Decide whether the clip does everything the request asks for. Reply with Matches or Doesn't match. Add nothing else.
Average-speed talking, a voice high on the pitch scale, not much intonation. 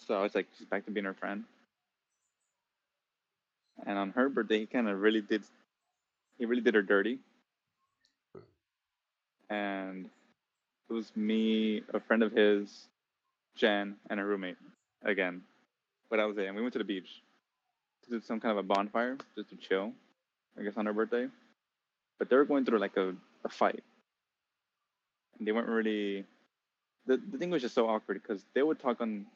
Doesn't match